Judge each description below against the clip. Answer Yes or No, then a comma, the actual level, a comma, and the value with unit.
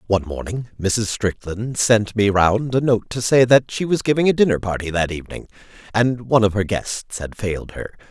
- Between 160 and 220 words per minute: Yes, fast, 205 wpm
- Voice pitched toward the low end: Yes, low, 110 Hz